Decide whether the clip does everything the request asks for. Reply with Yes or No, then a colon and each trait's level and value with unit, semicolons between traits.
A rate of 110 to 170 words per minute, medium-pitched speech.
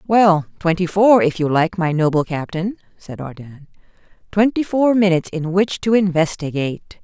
Yes: average, 155 wpm; medium, 180 Hz